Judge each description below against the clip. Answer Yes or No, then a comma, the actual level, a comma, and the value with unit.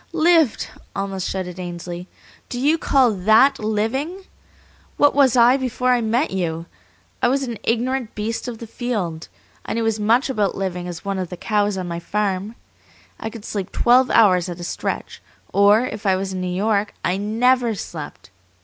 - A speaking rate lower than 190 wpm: Yes, average, 180 wpm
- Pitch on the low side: No, high, 210 Hz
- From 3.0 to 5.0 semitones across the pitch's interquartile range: Yes, average, 4.7 semitones